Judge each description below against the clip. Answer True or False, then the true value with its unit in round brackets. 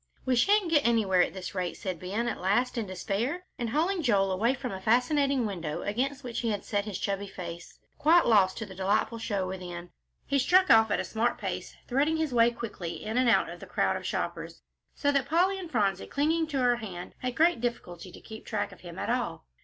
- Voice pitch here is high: True (230 Hz)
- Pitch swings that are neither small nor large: False (6.2 semitones)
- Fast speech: True (225 wpm)